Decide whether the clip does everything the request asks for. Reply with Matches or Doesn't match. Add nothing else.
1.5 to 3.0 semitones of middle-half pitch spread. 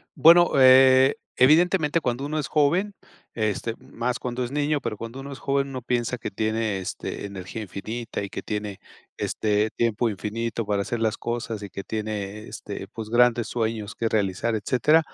Doesn't match